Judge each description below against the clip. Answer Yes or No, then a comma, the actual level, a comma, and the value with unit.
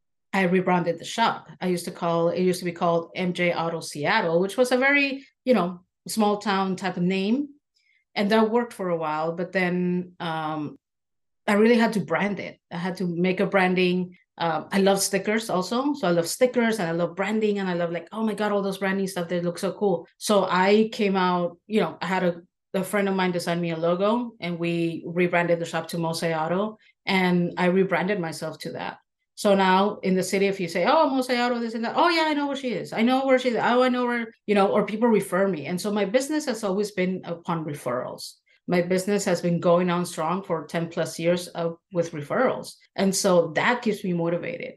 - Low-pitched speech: No, medium, 185 Hz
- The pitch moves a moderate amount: Yes, average, 3.5 semitones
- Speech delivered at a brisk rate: Yes, fast, 230 wpm